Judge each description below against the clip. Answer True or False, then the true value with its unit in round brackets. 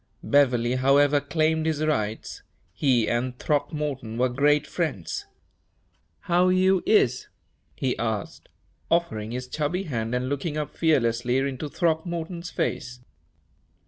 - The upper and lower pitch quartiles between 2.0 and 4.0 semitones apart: False (4.4 semitones)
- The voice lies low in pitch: False (145 Hz)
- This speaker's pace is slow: True (115 wpm)